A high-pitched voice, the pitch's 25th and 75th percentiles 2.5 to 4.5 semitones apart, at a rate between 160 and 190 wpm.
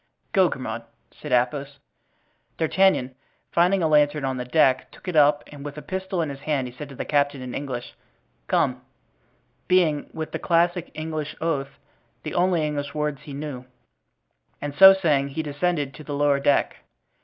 No: medium, 150 Hz; average, 2.8 semitones; average, 175 wpm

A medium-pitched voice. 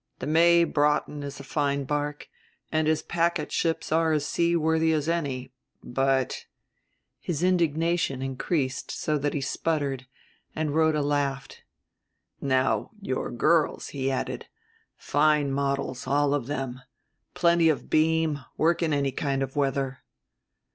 Yes: medium, 145 Hz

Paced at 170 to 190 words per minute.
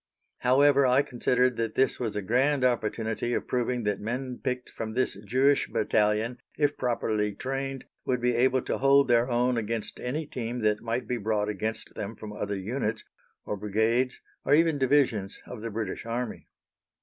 Yes: average, 175 wpm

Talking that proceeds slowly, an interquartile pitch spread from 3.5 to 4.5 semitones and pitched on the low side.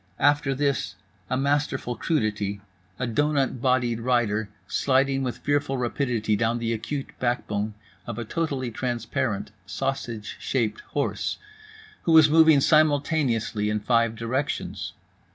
Yes: slow, 115 wpm; average, 4.0 semitones; low, 125 Hz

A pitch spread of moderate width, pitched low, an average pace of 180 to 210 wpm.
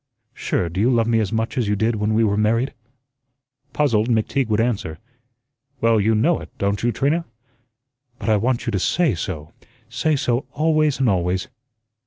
Yes: average, 3.7 semitones; low, 115 Hz; average, 185 wpm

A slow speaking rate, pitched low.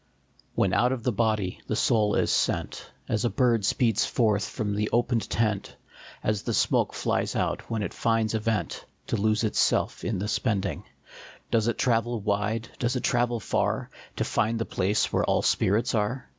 No: average, 185 wpm; low, 110 Hz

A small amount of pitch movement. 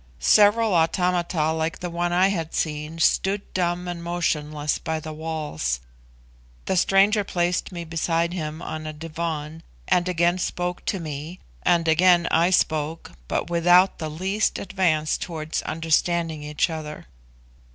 Yes: narrow, 2.3 semitones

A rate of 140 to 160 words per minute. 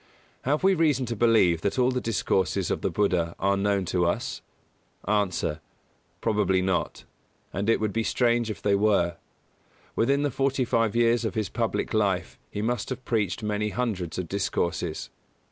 No: average, 170 wpm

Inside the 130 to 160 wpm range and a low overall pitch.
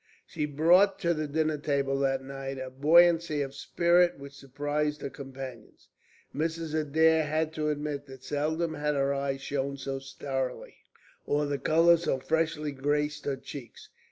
No: average, 155 wpm; medium, 145 Hz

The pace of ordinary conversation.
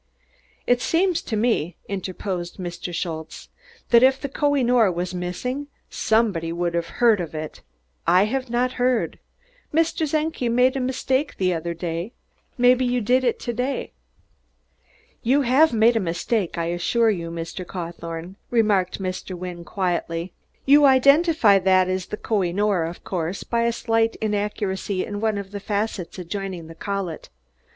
Yes: average, 160 wpm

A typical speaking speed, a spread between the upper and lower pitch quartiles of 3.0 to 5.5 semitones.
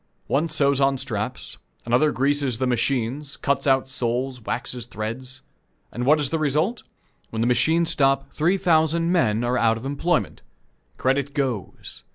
Yes: average, 155 wpm; average, 3.5 semitones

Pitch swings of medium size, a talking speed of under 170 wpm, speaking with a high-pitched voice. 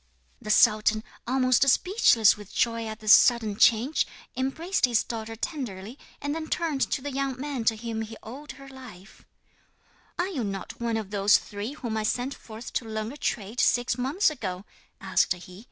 No: average, 3.9 semitones; average, 180 wpm; high, 230 Hz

